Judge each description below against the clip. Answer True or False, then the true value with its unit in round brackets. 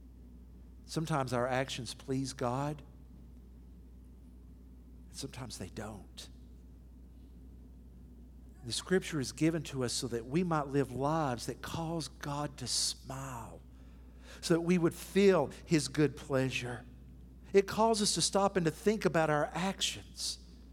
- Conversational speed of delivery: False (130 wpm)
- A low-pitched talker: True (120 Hz)